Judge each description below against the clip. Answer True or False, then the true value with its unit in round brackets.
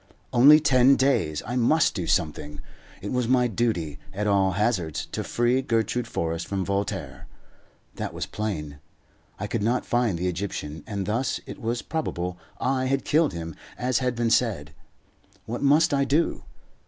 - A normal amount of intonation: False (6.0 semitones)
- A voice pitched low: True (115 Hz)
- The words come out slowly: False (165 wpm)